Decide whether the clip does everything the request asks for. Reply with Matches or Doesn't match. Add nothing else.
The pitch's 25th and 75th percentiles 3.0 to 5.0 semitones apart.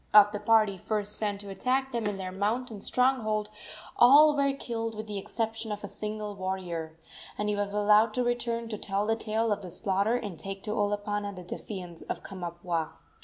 Doesn't match